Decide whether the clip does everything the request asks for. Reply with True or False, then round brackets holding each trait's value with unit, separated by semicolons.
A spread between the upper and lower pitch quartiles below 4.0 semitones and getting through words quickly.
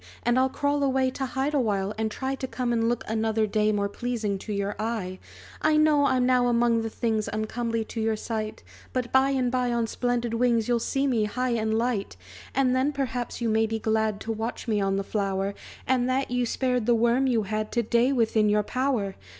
True (2.8 semitones; 215 wpm)